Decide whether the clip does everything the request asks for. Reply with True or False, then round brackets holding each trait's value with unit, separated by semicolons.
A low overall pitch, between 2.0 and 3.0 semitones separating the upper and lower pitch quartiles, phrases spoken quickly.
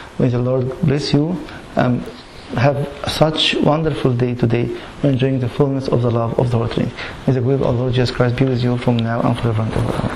True (125 Hz; 2.5 semitones; 225 wpm)